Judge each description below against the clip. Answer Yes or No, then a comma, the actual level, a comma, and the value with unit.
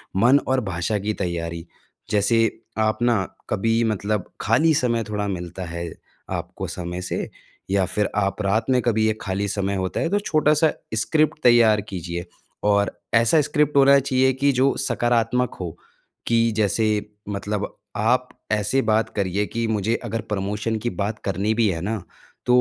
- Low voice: Yes, low, 110 Hz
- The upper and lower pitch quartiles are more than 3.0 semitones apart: Yes, average, 3.5 semitones